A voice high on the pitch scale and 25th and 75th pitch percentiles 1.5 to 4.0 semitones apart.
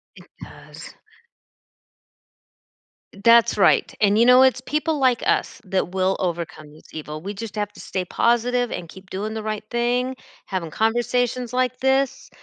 No: high, 225 Hz; average, 4.7 semitones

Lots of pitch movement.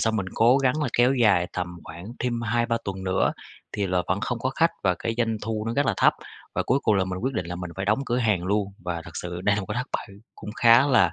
No: average, 4.4 semitones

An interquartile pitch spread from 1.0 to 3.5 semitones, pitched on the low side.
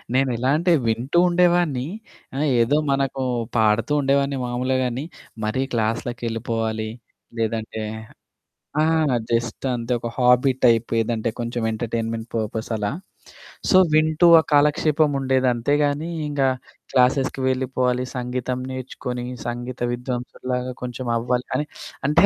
Yes: average, 2.8 semitones; low, 125 Hz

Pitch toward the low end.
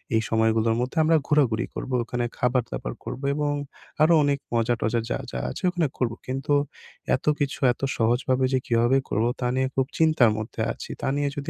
Yes: low, 125 Hz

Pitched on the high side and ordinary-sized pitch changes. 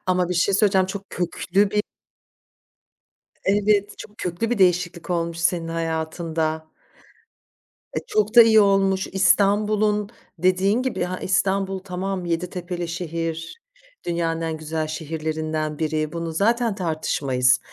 No: medium, 180 Hz; average, 3.3 semitones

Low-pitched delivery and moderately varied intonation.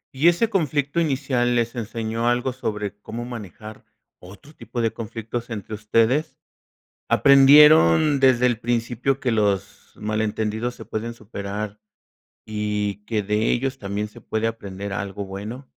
Yes: low, 115 Hz; average, 3.3 semitones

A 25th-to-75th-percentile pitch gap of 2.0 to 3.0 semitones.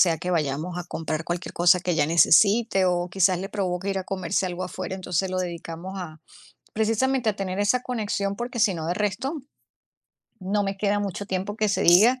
Yes: average, 2.7 semitones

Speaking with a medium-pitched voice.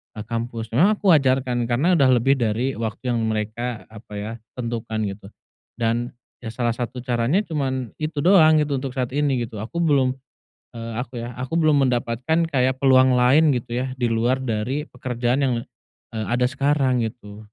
No: low, 125 Hz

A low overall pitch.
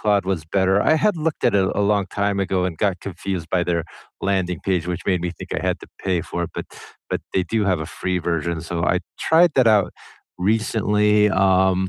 Yes: very low, 95 Hz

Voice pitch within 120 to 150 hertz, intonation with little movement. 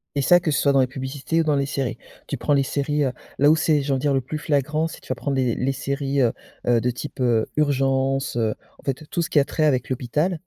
Yes: medium, 140 Hz; narrow, 2.2 semitones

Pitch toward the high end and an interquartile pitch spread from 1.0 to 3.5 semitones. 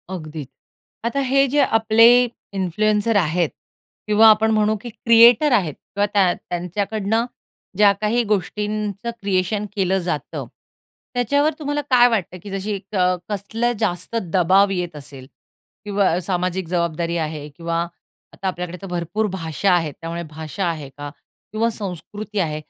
No: high, 195 Hz; average, 4.0 semitones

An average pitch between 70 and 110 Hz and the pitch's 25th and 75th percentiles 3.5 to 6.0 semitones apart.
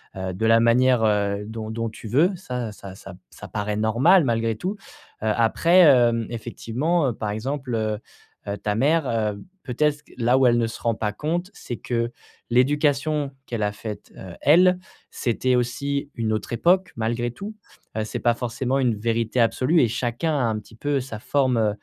No: low, 120 Hz; average, 4.1 semitones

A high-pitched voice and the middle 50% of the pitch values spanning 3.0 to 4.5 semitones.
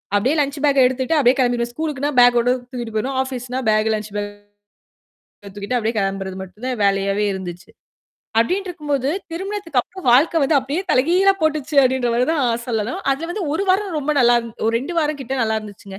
No: very high, 255 Hz; average, 5.3 semitones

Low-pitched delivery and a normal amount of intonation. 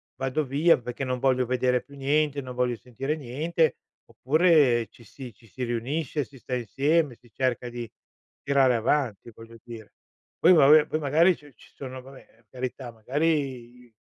Yes: low, 130 Hz; average, 3.4 semitones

